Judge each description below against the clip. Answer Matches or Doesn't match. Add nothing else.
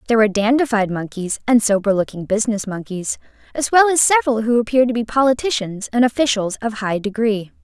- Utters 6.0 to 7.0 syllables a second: Matches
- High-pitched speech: Matches